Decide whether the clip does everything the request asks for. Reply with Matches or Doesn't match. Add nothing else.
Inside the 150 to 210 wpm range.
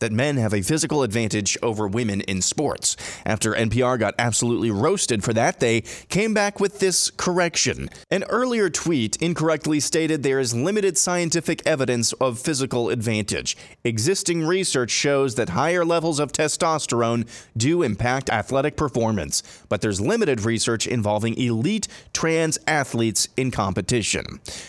Doesn't match